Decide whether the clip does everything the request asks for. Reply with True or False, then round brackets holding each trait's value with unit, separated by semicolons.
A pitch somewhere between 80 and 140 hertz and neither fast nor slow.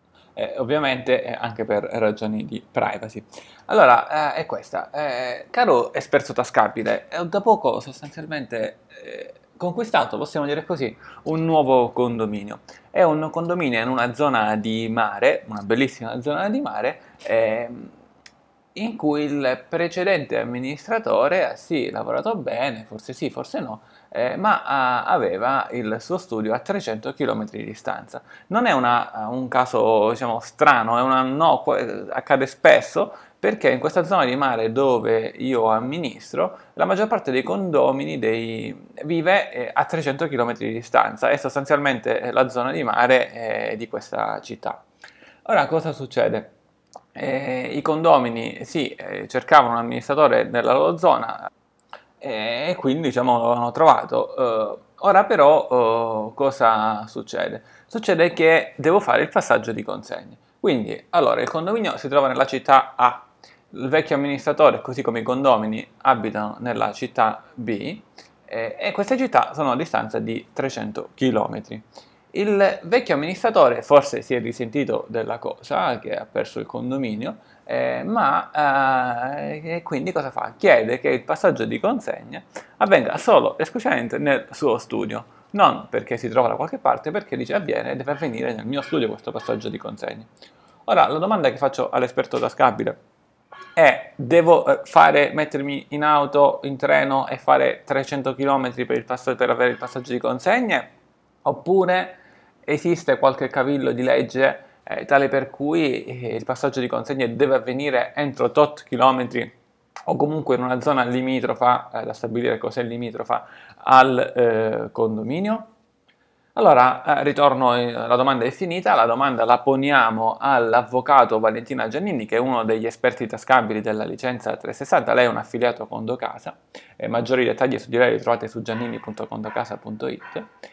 True (135 Hz; 150 wpm)